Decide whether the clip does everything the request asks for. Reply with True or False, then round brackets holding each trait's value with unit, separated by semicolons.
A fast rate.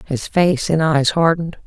False (180 wpm)